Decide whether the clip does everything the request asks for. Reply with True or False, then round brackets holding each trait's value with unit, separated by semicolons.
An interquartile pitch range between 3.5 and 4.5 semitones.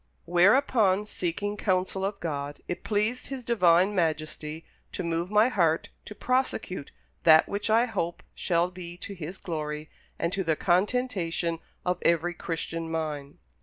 True (3.8 semitones)